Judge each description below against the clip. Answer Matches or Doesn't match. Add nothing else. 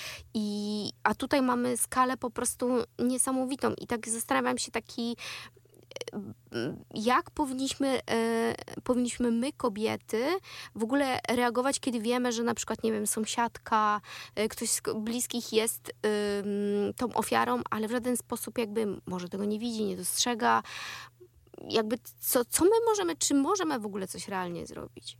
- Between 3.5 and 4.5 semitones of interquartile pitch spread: Doesn't match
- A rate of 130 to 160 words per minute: Matches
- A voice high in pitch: Matches